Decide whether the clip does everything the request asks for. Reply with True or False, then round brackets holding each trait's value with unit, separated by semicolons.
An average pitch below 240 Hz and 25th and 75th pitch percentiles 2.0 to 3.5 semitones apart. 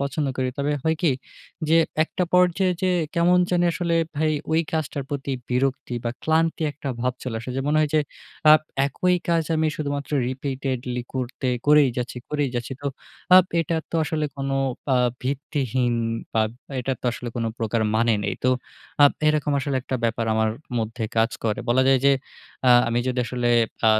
False (140 Hz; 3.9 semitones)